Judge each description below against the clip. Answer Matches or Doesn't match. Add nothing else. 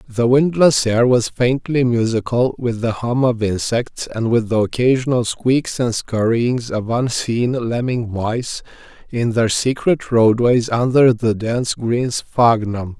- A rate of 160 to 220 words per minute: Doesn't match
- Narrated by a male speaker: Matches